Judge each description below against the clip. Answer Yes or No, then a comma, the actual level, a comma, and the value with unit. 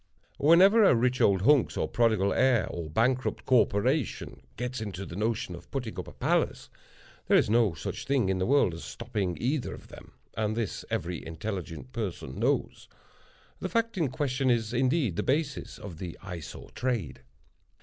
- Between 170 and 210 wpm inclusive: Yes, average, 175 wpm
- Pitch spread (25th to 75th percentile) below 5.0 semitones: No, wide, 5.4 semitones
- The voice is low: Yes, low, 115 Hz